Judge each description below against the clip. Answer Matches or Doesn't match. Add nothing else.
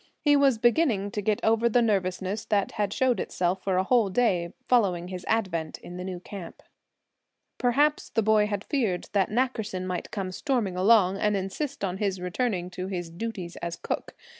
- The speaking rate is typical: Matches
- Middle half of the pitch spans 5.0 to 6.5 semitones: Doesn't match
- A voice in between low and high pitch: Doesn't match